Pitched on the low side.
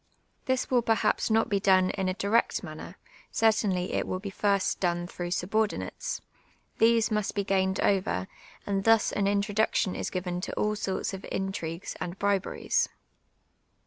No: high, 195 Hz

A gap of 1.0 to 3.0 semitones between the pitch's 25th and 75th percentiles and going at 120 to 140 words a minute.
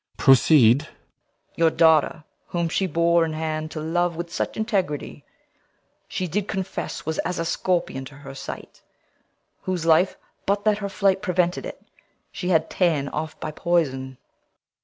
No: average, 2.7 semitones; average, 155 wpm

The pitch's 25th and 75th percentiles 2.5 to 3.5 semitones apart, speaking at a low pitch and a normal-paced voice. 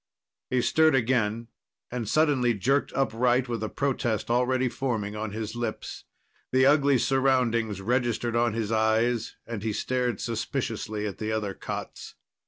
Yes: average, 2.8 semitones; low, 120 Hz; average, 145 wpm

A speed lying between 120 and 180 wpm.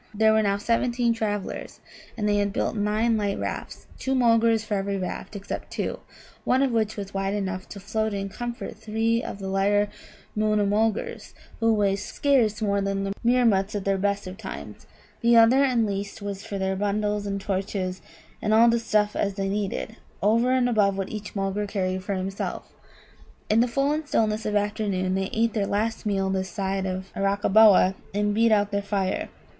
No: average, 190 wpm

